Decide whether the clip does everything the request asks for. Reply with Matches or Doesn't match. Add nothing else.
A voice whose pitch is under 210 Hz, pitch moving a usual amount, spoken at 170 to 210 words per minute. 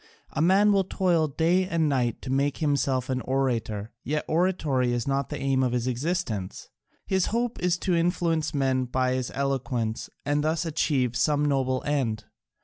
Matches